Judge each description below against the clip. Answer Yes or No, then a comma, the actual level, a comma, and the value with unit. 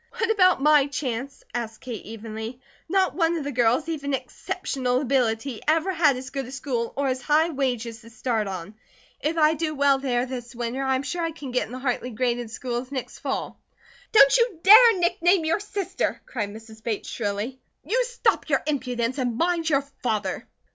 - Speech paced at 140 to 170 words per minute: No, average, 190 wpm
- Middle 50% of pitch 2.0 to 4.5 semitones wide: No, average, 4.9 semitones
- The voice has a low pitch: No, very high, 265 Hz